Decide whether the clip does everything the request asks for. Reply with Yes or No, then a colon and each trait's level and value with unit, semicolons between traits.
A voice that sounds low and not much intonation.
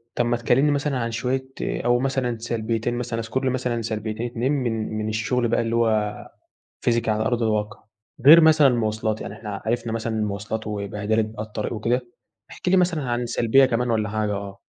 Yes: low, 115 Hz; narrow, 2.2 semitones